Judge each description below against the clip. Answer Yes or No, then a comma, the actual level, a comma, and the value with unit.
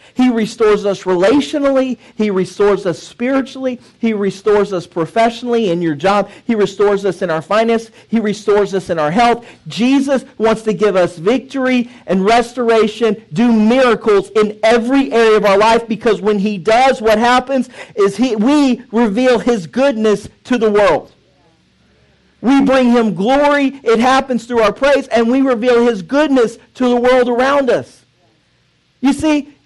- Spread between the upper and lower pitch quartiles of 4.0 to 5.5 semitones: No, average, 3.5 semitones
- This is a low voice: No, high, 230 Hz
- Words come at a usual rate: Yes, average, 160 wpm